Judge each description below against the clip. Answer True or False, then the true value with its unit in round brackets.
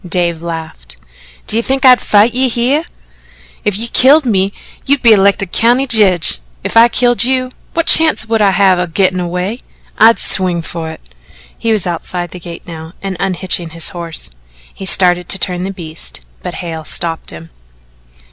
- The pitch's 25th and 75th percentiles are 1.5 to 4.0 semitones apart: False (5.2 semitones)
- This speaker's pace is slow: False (175 wpm)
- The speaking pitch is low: False (190 Hz)